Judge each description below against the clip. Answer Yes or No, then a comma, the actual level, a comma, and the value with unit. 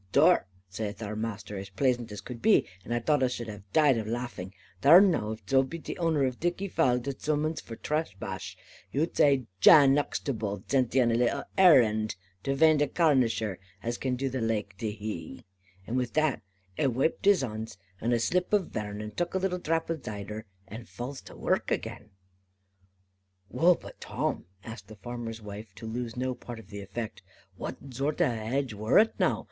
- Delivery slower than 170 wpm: No, average, 200 wpm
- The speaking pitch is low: Yes, low, 120 Hz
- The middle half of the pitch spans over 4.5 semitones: Yes, average, 5.1 semitones